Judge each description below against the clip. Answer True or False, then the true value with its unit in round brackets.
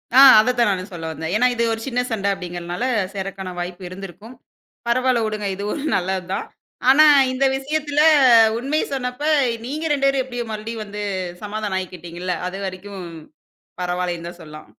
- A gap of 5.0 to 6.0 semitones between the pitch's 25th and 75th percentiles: True (5.6 semitones)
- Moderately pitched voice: False (200 Hz)